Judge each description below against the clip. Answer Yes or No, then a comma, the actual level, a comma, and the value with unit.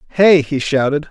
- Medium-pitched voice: Yes, medium, 150 Hz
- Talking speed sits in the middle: Yes, average, 165 wpm